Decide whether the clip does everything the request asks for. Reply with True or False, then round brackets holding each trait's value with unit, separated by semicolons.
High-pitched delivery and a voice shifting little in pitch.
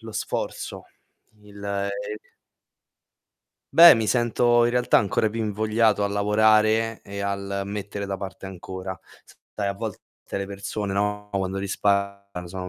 False (100 Hz; 1.7 semitones)